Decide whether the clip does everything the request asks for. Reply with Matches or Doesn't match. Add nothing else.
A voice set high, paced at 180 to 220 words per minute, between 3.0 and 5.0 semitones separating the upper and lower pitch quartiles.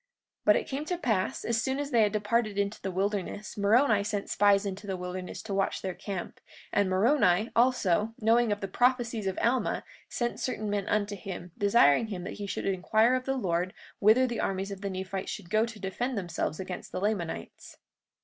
Matches